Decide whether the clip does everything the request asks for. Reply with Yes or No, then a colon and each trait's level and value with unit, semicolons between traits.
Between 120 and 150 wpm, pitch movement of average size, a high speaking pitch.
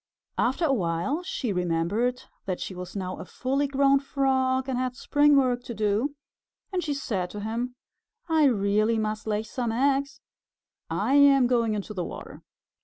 No: average, 170 wpm; average, 4.7 semitones; high, 245 Hz